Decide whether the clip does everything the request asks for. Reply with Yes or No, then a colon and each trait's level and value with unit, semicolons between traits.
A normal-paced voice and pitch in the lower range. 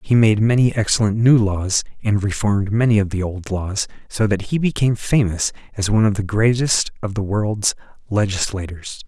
Yes: average, 180 wpm; low, 105 Hz